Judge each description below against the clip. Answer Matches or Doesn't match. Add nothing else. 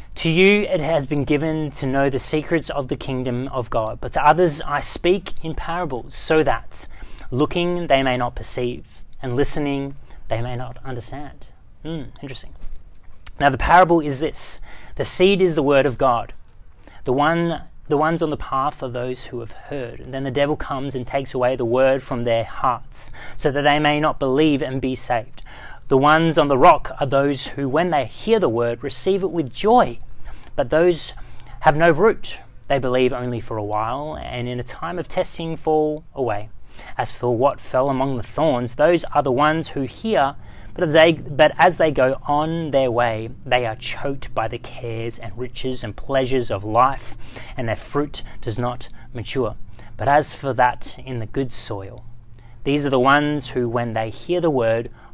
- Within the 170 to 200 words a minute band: Matches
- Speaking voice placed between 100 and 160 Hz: Matches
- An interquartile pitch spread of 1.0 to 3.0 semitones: Doesn't match